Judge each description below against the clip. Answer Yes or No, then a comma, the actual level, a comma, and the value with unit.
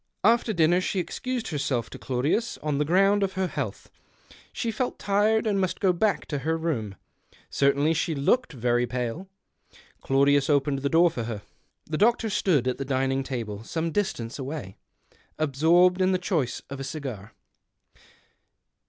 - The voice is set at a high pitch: No, medium, 155 Hz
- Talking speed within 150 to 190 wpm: Yes, average, 160 wpm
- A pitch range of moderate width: No, wide, 6.1 semitones